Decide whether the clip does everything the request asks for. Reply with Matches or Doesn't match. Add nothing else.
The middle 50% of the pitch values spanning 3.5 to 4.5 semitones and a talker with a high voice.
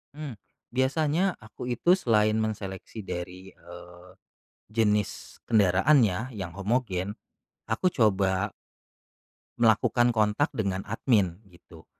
Doesn't match